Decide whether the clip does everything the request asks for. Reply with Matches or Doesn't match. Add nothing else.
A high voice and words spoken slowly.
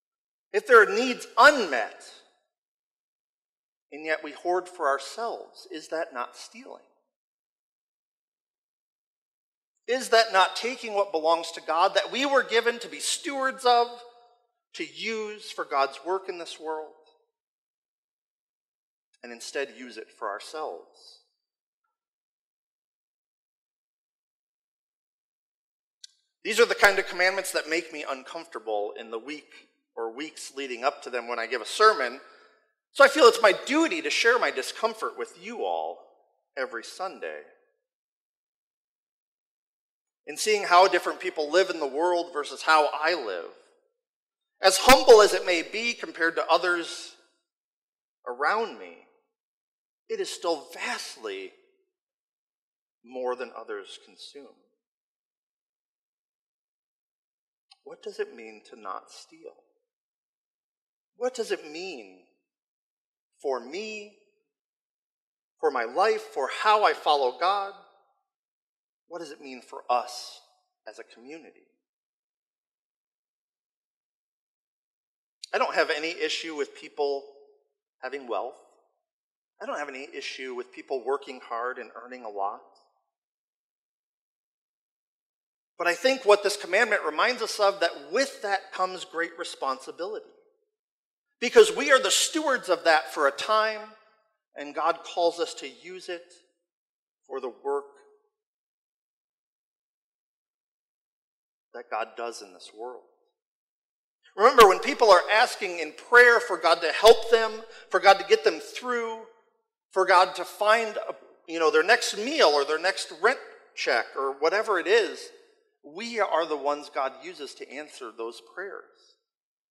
Matches